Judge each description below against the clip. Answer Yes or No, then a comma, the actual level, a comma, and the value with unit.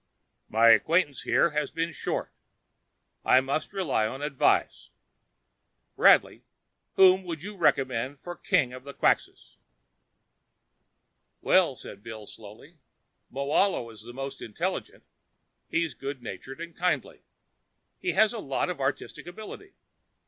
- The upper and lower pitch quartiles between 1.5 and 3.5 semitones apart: No, wide, 5.4 semitones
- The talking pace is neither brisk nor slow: No, slow, 125 wpm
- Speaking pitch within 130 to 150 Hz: Yes, medium, 140 Hz